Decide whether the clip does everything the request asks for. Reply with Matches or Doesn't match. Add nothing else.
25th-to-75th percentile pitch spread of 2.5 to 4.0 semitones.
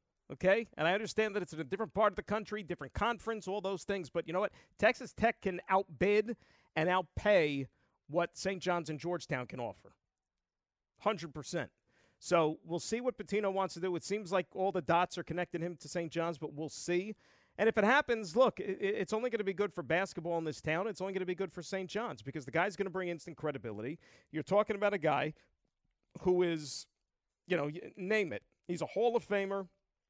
Matches